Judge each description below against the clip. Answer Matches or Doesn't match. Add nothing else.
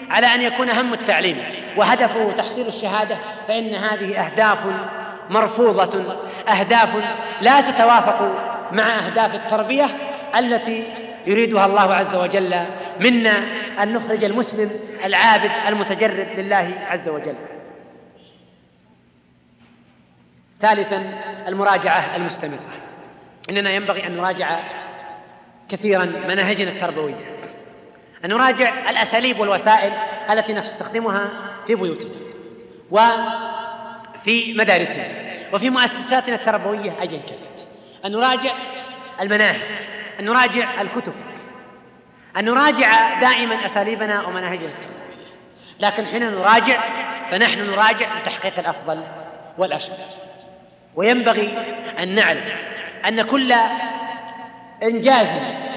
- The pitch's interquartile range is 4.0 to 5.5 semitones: Doesn't match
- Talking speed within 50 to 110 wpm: Matches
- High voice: Matches